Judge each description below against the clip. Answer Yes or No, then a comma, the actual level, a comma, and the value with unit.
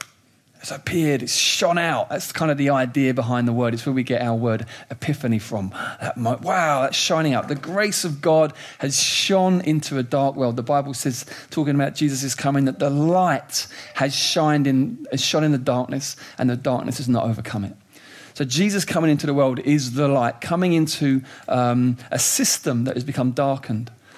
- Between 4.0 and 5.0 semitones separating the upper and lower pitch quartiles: No, average, 3.3 semitones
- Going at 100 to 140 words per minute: No, average, 195 wpm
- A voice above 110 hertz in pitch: Yes, medium, 140 Hz